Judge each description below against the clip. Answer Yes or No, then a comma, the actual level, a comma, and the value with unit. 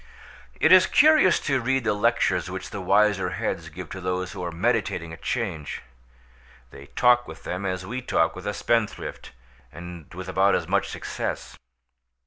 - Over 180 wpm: No, average, 170 wpm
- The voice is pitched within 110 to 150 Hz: No, very low, 95 Hz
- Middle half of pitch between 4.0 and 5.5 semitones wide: Yes, average, 4.6 semitones